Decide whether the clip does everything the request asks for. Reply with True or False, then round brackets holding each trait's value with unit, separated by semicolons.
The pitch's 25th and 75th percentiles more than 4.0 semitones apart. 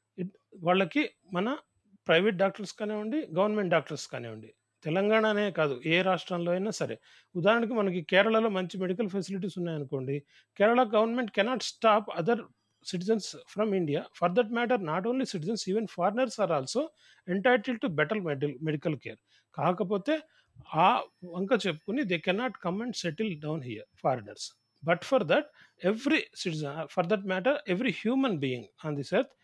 True (4.6 semitones)